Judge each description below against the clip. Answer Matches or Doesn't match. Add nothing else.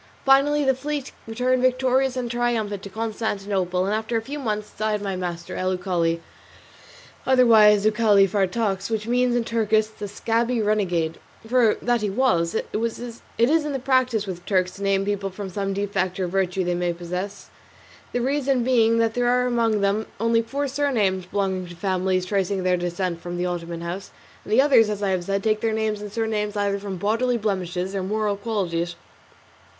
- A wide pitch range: Doesn't match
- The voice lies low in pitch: Doesn't match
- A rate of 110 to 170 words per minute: Doesn't match